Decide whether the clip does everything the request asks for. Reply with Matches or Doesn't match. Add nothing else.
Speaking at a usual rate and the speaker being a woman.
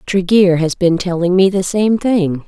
Matches